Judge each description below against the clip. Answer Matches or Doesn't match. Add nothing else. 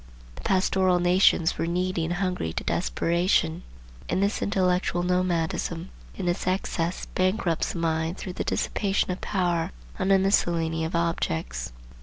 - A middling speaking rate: Matches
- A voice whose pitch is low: Doesn't match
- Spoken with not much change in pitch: Matches